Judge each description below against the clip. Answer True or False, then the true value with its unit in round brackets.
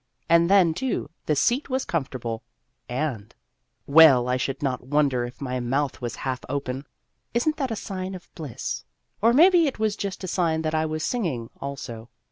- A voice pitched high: False (155 Hz)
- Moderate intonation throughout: False (7.1 semitones)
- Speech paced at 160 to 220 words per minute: True (185 wpm)